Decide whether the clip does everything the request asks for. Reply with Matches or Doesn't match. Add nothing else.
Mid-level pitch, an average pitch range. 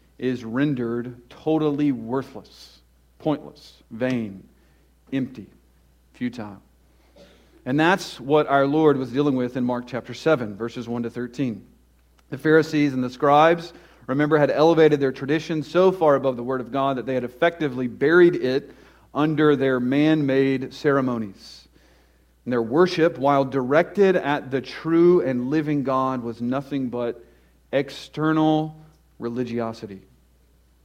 Doesn't match